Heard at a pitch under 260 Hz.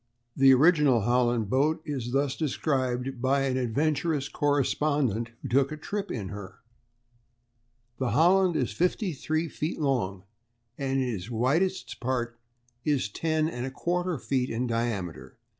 Yes: low, 135 Hz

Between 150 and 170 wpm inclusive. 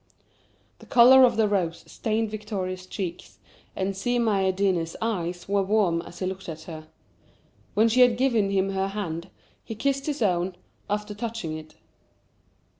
Yes: average, 155 wpm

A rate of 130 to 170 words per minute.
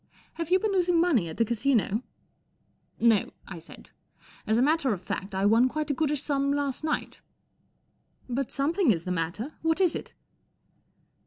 No: average, 190 wpm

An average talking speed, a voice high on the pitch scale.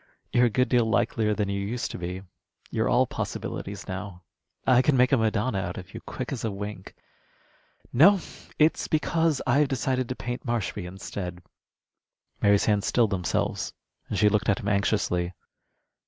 No: average, 170 wpm; low, 110 Hz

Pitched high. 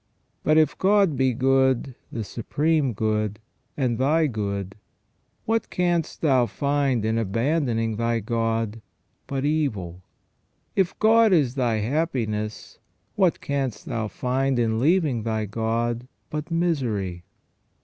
No: low, 125 Hz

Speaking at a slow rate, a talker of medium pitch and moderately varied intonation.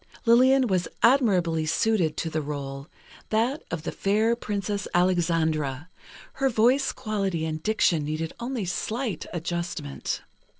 No: slow, 125 wpm; medium, 180 Hz; wide, 5.9 semitones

